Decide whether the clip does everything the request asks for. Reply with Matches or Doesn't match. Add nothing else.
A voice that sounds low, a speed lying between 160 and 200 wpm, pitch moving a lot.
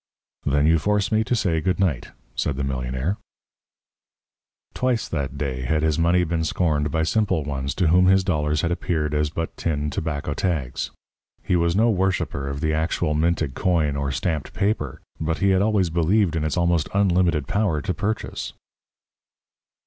Doesn't match